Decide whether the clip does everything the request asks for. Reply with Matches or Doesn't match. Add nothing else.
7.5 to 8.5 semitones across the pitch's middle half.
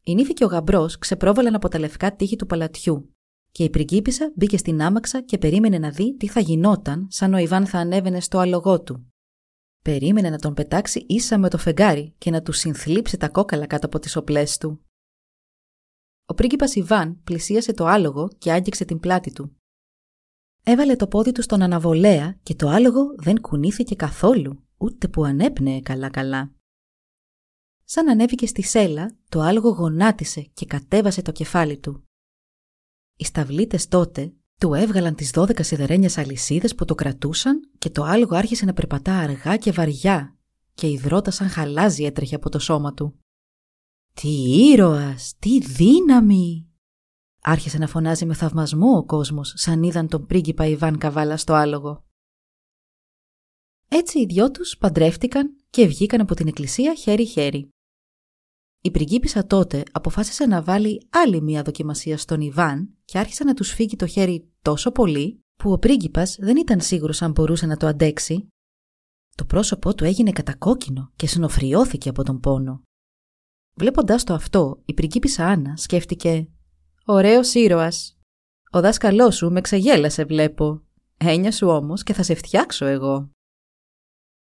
Doesn't match